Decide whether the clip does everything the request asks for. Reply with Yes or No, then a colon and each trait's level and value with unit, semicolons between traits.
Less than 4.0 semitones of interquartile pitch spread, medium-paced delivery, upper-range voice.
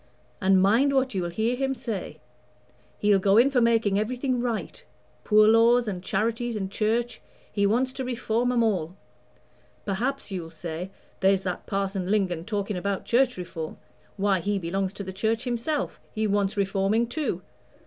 Yes: average, 3.6 semitones; average, 160 wpm; high, 210 Hz